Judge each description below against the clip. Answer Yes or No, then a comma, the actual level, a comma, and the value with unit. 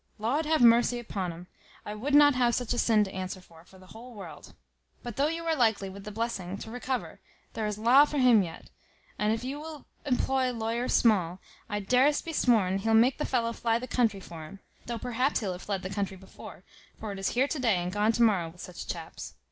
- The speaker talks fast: Yes, fast, 235 wpm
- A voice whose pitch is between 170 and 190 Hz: No, high, 225 Hz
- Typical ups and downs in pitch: Yes, average, 4.5 semitones